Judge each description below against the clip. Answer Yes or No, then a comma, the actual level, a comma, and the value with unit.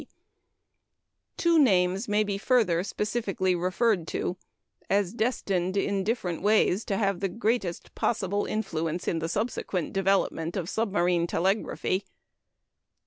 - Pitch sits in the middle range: No, high, 195 Hz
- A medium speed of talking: No, slow, 125 wpm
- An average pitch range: Yes, average, 3.2 semitones